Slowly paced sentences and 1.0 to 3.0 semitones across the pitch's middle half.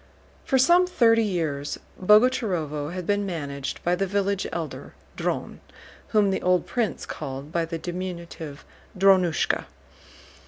No: slow, 125 wpm; average, 4.2 semitones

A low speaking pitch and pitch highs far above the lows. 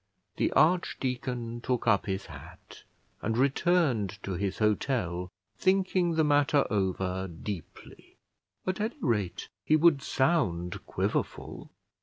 Yes: low, 120 Hz; wide, 8.4 semitones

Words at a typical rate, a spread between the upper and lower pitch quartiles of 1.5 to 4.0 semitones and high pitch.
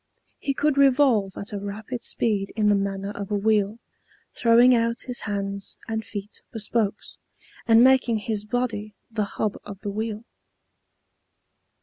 Yes: average, 150 wpm; narrow, 2.5 semitones; high, 215 Hz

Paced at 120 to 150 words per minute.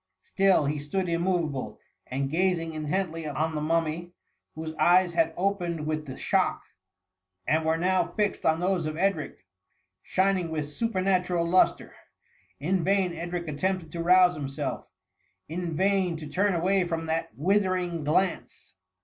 Yes: average, 145 wpm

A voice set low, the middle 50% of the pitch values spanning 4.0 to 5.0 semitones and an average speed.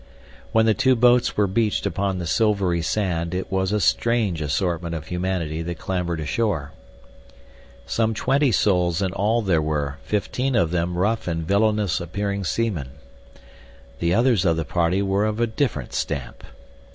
Yes: very low, 95 Hz; average, 4.4 semitones; average, 155 wpm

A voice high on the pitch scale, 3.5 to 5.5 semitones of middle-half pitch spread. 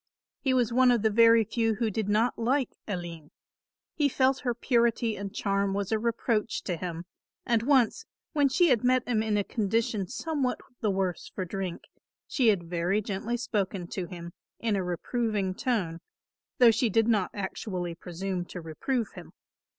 Yes: high, 215 Hz; average, 4.1 semitones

